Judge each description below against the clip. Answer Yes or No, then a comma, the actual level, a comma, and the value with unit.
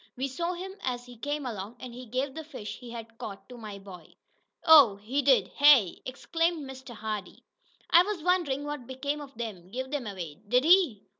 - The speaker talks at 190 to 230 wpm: Yes, average, 200 wpm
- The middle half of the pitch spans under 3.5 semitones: No, average, 4.9 semitones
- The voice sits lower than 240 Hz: No, very high, 255 Hz